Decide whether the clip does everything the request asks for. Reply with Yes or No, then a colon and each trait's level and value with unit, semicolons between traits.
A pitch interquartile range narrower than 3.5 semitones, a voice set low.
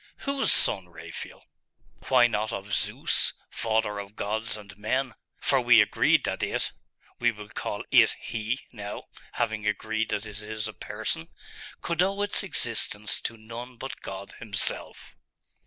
Yes: narrow, 2.5 semitones; low, 110 Hz